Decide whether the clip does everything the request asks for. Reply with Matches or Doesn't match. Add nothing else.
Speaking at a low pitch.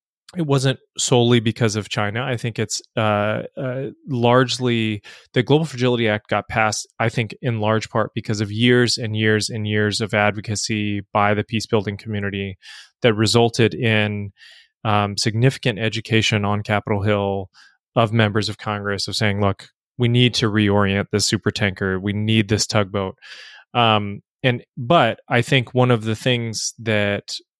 Matches